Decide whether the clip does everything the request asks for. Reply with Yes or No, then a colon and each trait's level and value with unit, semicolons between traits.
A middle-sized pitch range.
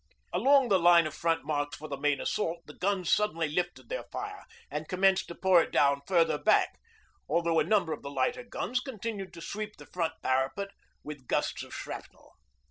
Yes: average, 5.0 semitones